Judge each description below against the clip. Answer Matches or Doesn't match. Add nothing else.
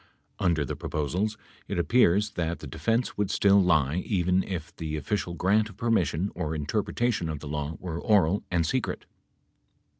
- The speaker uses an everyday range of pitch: Matches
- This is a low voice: Matches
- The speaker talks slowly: Doesn't match